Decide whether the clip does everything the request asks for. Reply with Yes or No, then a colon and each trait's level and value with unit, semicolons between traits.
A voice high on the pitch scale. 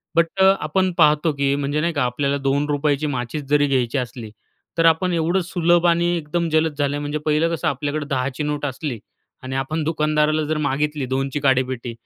No: medium, 150 Hz